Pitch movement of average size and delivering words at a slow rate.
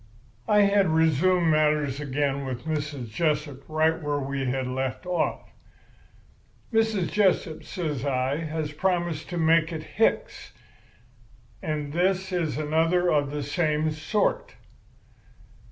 Yes: average, 3.2 semitones; slow, 120 wpm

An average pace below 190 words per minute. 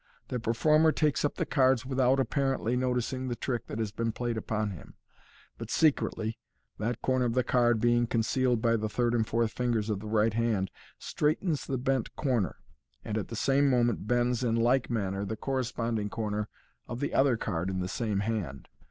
No: average, 195 wpm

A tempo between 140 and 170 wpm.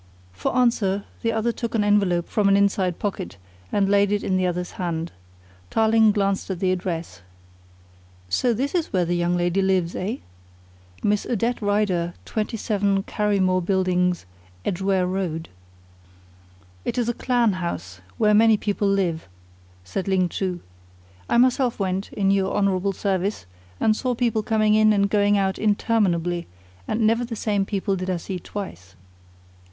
Yes: average, 155 wpm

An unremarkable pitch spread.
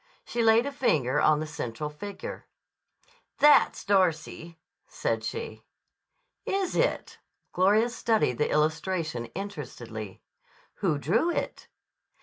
No: wide, 7.3 semitones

